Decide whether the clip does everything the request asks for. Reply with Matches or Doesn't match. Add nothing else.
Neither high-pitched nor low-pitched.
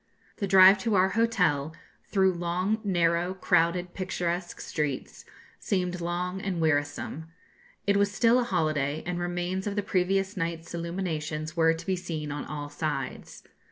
Matches